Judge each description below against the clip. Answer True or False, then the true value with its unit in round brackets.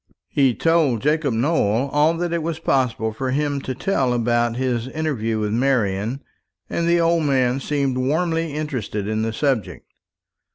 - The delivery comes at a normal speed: True (160 wpm)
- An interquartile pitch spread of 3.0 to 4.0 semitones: False (4.7 semitones)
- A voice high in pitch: False (135 Hz)